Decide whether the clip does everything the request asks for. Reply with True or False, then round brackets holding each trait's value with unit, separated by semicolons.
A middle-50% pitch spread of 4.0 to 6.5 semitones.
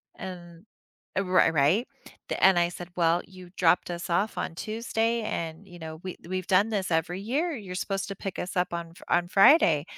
False (2.5 semitones)